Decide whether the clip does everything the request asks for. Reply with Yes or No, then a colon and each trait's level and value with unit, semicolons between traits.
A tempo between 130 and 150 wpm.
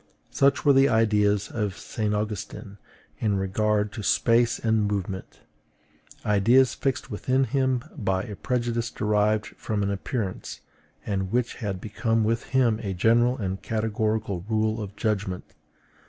Yes: average, 140 wpm